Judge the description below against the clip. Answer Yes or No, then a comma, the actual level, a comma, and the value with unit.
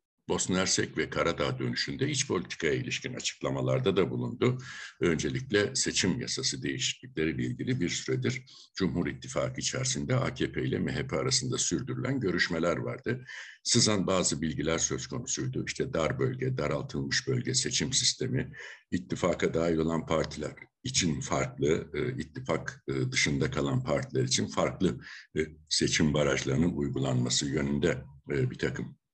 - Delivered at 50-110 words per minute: No, average, 120 wpm